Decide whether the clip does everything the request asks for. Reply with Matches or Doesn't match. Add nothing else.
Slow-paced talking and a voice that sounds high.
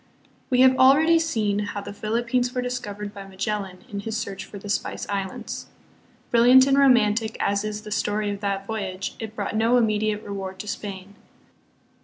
Doesn't match